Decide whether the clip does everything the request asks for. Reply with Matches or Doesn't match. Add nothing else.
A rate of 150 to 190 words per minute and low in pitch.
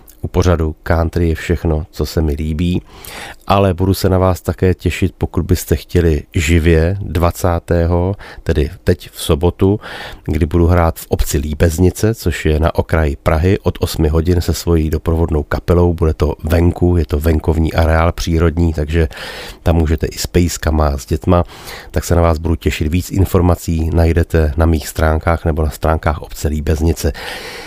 Matches